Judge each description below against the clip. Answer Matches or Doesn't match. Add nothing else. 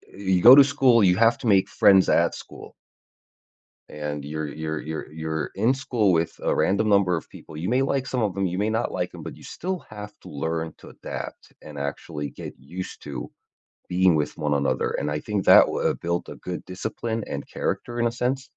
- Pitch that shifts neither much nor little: Doesn't match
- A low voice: Matches